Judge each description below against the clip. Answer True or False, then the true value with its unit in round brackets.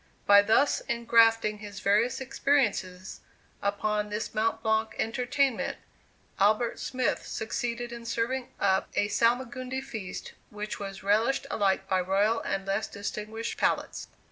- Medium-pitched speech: False (220 Hz)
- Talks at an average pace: False (125 wpm)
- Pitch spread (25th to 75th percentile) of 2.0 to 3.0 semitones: True (2.7 semitones)